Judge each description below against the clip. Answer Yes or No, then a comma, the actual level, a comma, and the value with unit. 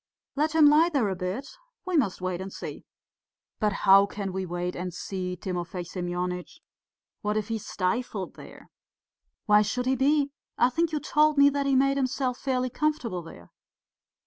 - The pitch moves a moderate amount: No, wide, 7.2 semitones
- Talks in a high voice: Yes, high, 215 Hz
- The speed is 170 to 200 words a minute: Yes, average, 175 wpm